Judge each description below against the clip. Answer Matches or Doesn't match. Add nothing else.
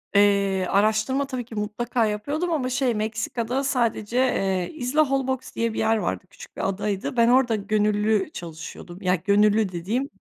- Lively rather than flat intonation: Doesn't match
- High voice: Matches